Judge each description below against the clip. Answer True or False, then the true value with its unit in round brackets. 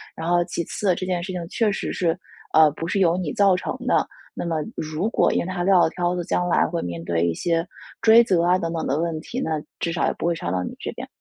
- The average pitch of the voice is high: False (170 Hz)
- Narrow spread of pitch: True (2.3 semitones)